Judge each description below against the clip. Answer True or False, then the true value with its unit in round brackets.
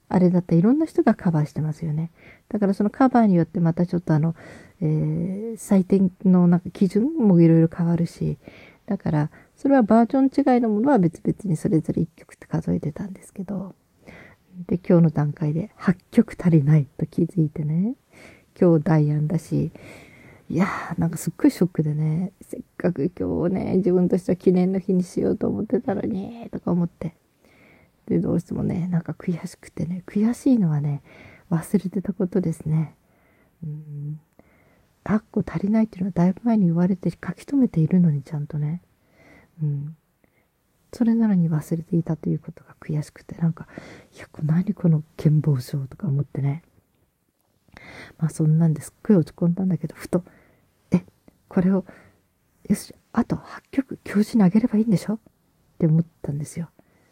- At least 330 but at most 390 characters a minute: True (345 characters per minute)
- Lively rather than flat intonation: False (4.0 semitones)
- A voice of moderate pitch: True (175 Hz)